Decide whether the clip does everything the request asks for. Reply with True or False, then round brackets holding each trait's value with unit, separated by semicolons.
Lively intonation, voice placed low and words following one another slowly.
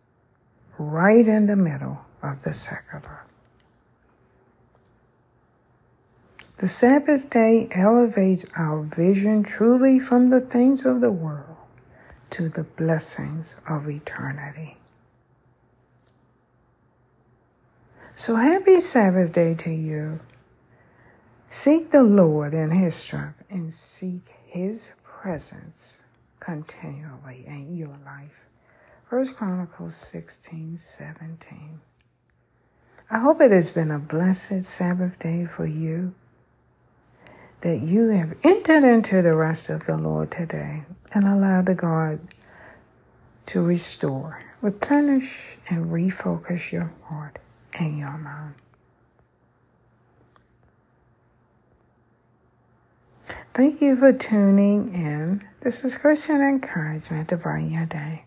False (7.5 semitones; 165 Hz; 100 wpm)